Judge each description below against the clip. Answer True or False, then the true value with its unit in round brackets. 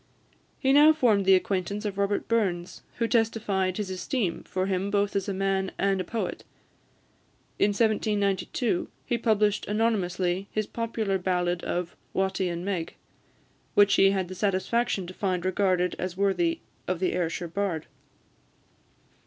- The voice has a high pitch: True (195 Hz)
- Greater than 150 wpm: False (145 wpm)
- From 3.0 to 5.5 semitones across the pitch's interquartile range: False (2.4 semitones)